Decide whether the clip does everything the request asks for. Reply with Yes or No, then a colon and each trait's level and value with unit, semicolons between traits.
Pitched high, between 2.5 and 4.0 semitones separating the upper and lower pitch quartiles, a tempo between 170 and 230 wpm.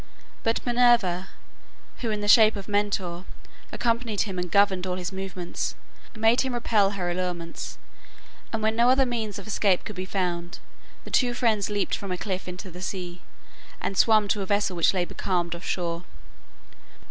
Yes: high, 195 Hz; average, 3.4 semitones; average, 175 wpm